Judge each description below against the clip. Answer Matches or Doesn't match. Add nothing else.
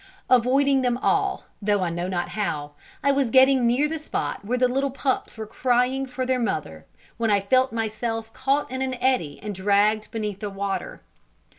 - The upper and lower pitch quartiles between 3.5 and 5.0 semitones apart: Matches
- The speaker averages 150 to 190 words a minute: Matches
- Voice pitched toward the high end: Matches